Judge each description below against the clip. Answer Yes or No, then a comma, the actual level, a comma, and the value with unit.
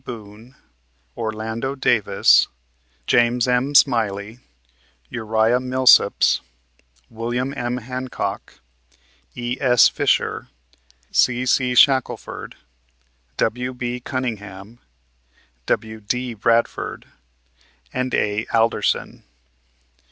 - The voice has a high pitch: No, low, 120 Hz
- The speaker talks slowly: Yes, slow, 65 wpm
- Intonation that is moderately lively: No, narrow, 2.3 semitones